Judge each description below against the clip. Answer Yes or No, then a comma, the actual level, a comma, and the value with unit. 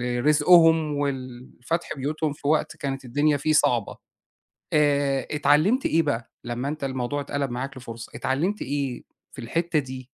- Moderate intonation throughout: Yes, average, 3.0 semitones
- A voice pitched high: No, medium, 140 Hz